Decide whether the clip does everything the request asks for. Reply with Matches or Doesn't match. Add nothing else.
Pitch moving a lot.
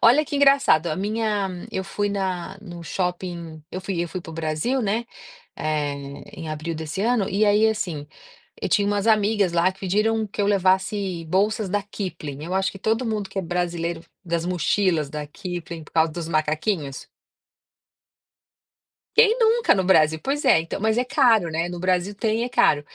Doesn't match